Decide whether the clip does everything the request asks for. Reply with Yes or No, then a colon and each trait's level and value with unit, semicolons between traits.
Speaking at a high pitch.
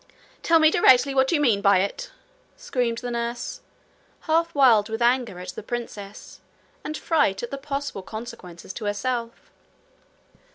Yes: high, 240 Hz